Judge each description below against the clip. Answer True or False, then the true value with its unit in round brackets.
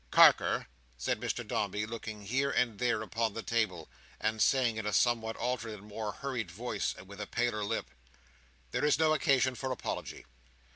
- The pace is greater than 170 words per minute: True (180 wpm)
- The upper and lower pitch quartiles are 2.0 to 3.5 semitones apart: True (2.9 semitones)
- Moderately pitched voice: False (110 Hz)